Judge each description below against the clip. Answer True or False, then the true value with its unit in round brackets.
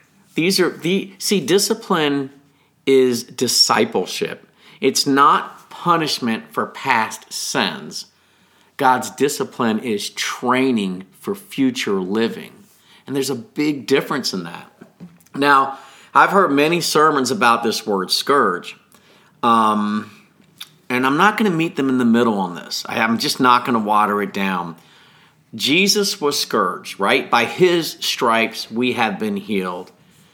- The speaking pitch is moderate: True (145 Hz)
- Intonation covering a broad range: True (8.0 semitones)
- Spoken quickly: False (135 wpm)